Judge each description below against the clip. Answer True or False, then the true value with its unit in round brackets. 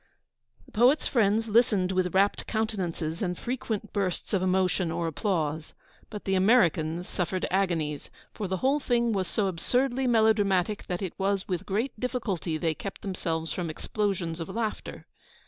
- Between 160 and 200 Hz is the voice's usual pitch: True (190 Hz)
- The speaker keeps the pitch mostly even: False (4.0 semitones)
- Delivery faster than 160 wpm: False (155 wpm)